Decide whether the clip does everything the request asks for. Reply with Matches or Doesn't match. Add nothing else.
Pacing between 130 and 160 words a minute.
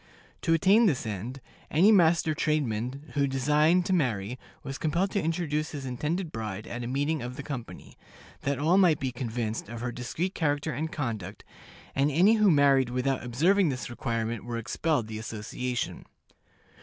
Doesn't match